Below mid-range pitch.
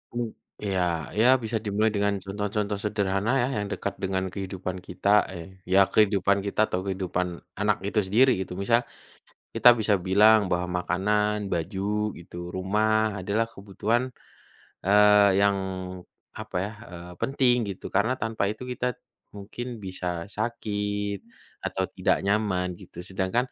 Yes: low, 100 Hz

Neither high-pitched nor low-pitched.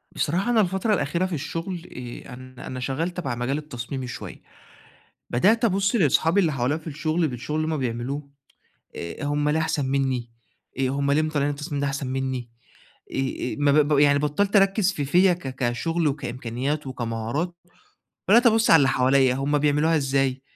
Yes: medium, 145 Hz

